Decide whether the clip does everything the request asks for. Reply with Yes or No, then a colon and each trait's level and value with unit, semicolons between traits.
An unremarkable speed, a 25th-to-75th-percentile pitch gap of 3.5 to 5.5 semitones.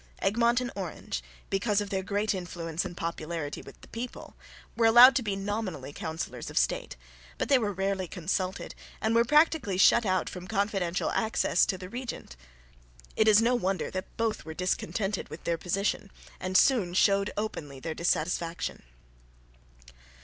Yes: average, 160 wpm; average, 3.8 semitones